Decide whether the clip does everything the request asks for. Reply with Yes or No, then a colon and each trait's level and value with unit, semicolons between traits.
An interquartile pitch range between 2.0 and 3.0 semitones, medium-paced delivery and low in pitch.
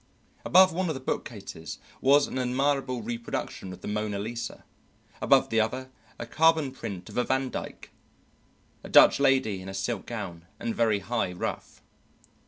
No: average, 4.6 semitones; average, 160 wpm; low, 120 Hz